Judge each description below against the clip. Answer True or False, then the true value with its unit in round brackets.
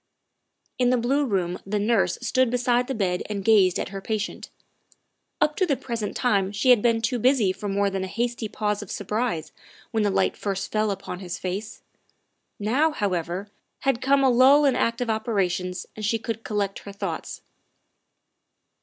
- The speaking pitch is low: False (215 Hz)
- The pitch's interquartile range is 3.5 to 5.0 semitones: True (3.8 semitones)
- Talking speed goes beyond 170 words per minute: True (180 wpm)